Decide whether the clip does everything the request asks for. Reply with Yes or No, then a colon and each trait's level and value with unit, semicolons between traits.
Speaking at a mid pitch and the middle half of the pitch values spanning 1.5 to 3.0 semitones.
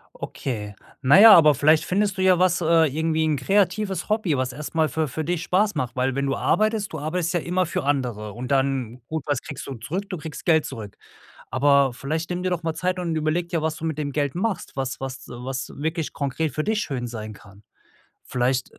No: medium, 155 Hz; average, 4.8 semitones